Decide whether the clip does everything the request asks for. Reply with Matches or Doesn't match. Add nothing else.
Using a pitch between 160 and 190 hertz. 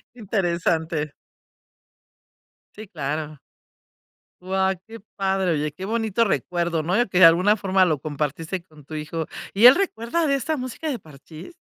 Matches